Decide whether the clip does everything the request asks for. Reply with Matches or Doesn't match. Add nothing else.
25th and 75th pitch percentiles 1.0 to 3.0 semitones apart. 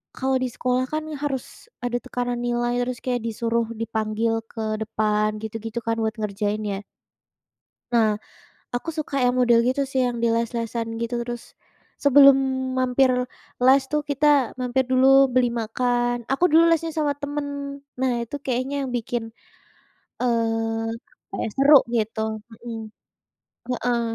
Matches